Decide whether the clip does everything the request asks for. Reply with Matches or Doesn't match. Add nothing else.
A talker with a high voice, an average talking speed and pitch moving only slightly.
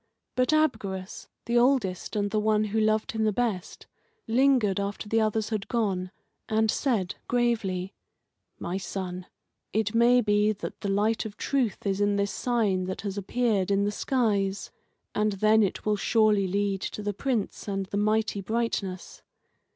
Matches